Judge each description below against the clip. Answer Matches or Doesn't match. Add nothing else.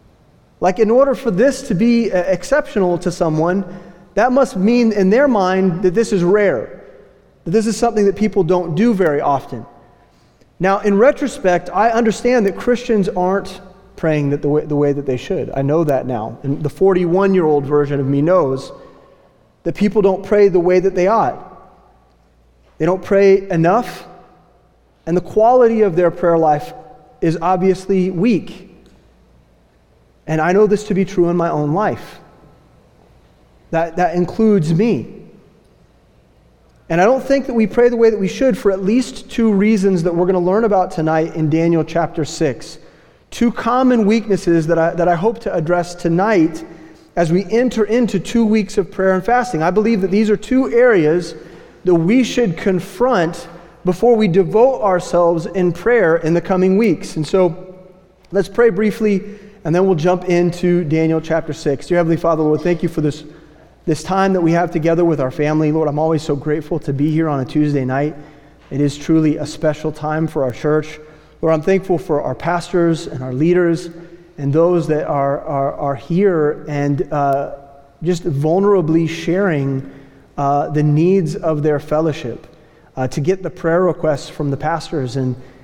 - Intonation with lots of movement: Doesn't match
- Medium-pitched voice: Matches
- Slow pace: Doesn't match